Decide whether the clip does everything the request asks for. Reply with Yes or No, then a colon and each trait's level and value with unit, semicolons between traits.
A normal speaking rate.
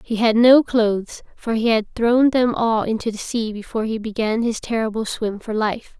No: fast, 210 wpm